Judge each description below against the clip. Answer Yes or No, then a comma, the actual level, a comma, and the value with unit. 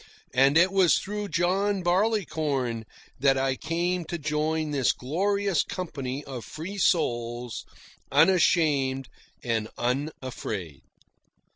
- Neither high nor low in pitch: Yes, medium, 155 Hz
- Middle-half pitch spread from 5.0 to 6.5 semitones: Yes, wide, 5.5 semitones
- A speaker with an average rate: No, slow, 105 wpm